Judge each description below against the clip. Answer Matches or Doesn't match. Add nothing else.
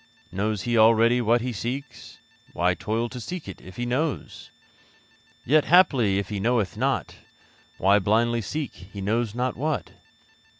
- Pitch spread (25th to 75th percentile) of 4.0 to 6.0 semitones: Doesn't match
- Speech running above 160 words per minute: Doesn't match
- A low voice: Matches